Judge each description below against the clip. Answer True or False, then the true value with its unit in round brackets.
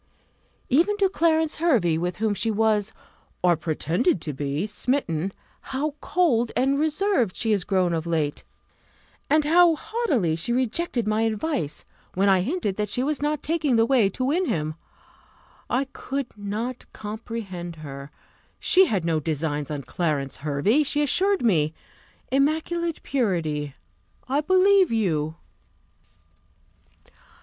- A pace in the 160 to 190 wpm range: False (135 wpm)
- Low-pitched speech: False (225 Hz)